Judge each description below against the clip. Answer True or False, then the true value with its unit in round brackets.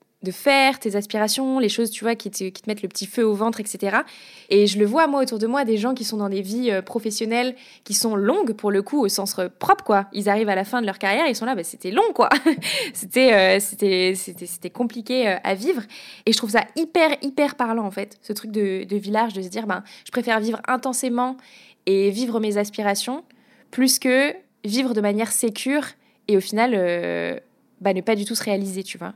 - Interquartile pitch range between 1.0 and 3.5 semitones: False (4.1 semitones)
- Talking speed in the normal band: False (245 wpm)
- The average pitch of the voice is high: True (220 Hz)